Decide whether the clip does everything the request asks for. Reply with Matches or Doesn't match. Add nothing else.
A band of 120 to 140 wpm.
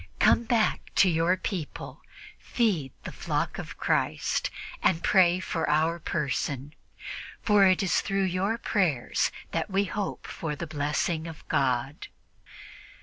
Matches